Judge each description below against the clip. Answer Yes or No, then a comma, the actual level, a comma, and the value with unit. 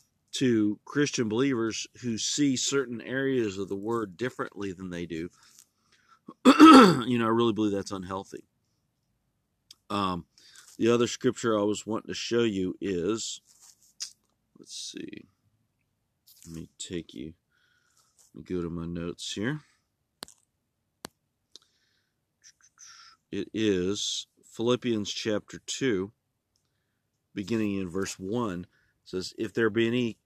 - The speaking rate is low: Yes, slow, 115 wpm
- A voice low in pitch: Yes, low, 110 Hz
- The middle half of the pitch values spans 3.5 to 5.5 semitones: Yes, average, 4.2 semitones